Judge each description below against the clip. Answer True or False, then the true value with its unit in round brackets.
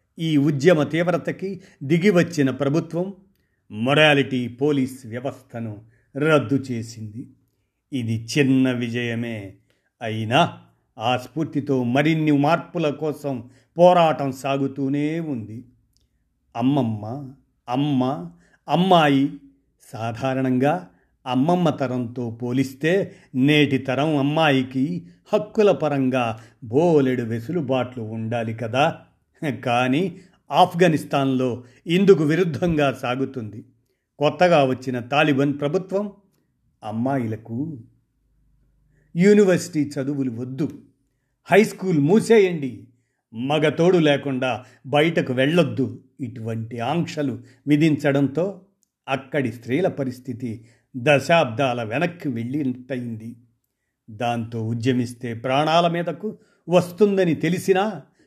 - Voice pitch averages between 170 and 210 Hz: False (135 Hz)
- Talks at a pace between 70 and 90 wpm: True (75 wpm)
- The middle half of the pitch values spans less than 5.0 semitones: True (4.4 semitones)